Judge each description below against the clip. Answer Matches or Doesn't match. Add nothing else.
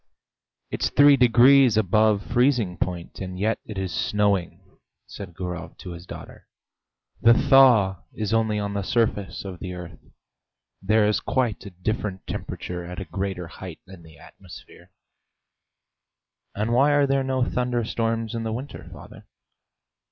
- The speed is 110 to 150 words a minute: Matches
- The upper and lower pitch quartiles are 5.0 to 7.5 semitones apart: Doesn't match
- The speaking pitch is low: Matches